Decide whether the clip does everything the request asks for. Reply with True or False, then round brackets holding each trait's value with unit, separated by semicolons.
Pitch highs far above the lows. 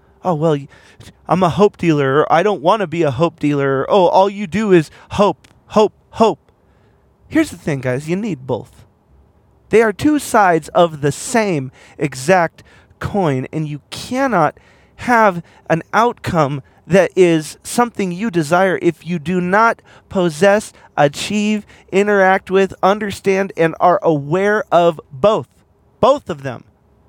True (5.7 semitones)